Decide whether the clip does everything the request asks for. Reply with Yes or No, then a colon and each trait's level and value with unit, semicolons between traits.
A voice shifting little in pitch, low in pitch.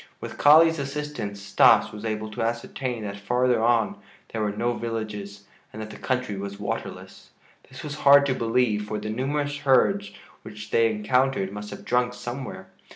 No: average, 3.9 semitones; low, 115 Hz